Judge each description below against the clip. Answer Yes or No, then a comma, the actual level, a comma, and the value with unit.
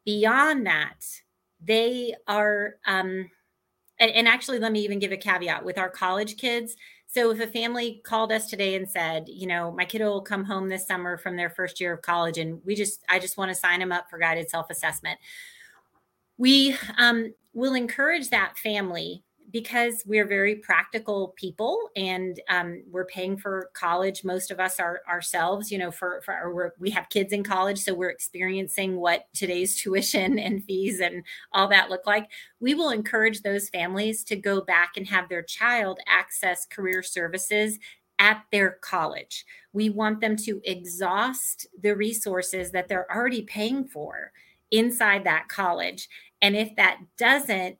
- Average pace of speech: Yes, average, 175 wpm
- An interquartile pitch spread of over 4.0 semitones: No, average, 3.2 semitones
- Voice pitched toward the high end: Yes, high, 195 Hz